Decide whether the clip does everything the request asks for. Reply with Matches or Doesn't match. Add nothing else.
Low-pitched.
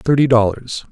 Matches